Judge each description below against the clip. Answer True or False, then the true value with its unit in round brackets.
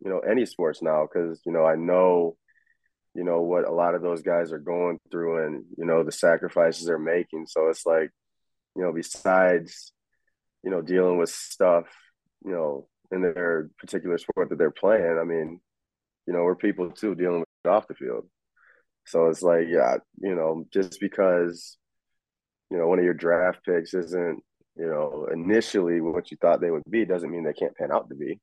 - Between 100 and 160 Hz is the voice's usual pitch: False (85 Hz)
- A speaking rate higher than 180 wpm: True (195 wpm)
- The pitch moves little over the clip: True (1.6 semitones)